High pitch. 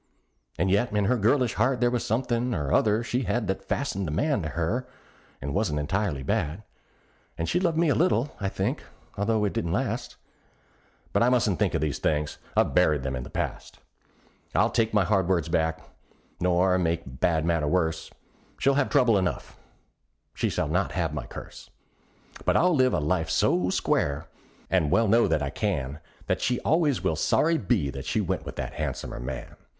No: very low, 95 Hz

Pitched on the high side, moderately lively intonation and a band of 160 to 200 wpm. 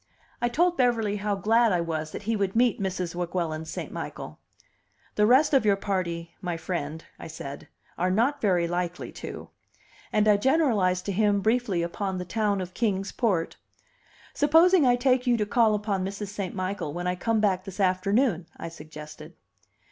Yes: high, 200 Hz; average, 4.2 semitones; average, 180 wpm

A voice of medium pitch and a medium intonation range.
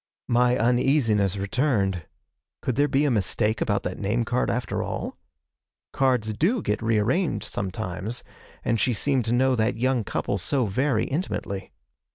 No: low, 115 Hz; average, 4.1 semitones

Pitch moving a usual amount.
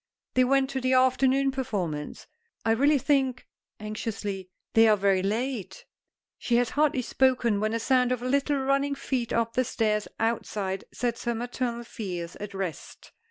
Yes: average, 3.8 semitones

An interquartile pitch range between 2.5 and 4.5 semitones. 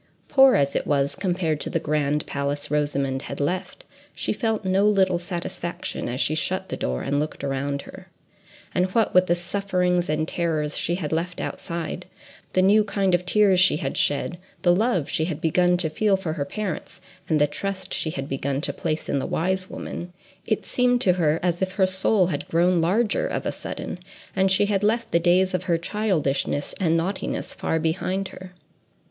Yes: average, 3.7 semitones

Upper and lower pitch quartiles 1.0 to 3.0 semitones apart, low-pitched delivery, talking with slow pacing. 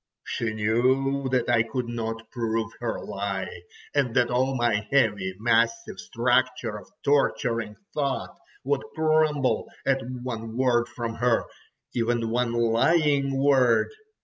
Yes: average, 2.7 semitones; low, 120 Hz; slow, 125 wpm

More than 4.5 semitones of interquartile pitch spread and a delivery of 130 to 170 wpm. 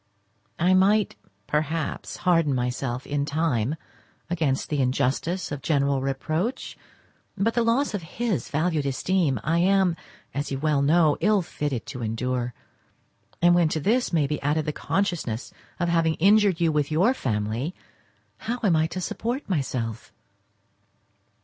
Yes: average, 5.0 semitones; average, 145 wpm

